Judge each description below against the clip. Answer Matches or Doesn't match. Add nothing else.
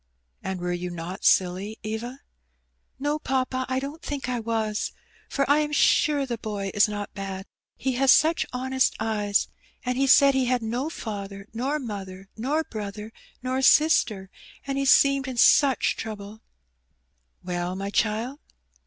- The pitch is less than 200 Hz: Doesn't match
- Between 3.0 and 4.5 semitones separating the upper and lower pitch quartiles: Doesn't match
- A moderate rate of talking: Matches